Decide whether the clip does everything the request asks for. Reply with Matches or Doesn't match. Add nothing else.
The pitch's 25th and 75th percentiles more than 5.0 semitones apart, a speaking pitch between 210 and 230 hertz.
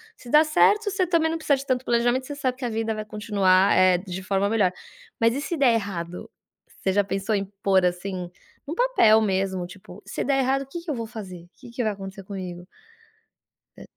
Matches